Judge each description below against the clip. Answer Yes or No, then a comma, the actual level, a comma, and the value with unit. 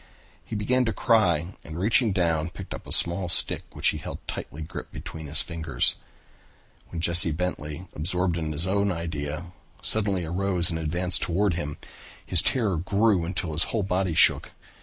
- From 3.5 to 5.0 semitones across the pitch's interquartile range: No, average, 3.1 semitones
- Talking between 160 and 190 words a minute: Yes, average, 170 wpm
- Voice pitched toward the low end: Yes, very low, 85 Hz